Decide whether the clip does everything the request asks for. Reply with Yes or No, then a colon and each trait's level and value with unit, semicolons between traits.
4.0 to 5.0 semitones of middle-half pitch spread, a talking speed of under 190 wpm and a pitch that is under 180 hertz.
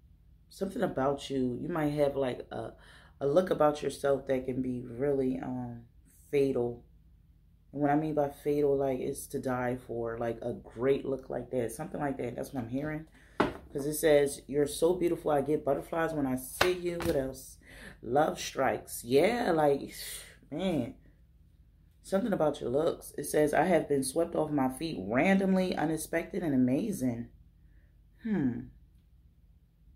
Yes: average, 4.3 semitones; average, 160 wpm; low, 135 Hz